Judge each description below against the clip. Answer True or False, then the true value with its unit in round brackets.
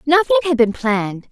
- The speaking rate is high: False (185 wpm)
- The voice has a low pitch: False (245 Hz)